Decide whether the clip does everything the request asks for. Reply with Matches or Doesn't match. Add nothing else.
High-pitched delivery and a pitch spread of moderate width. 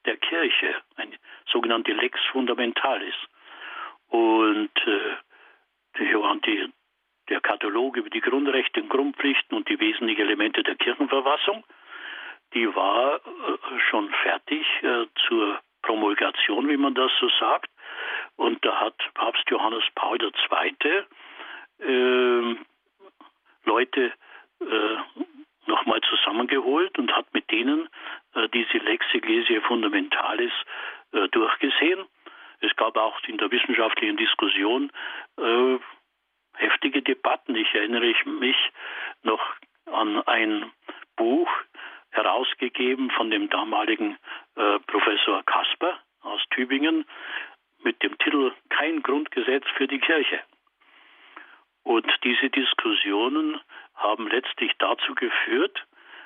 Doesn't match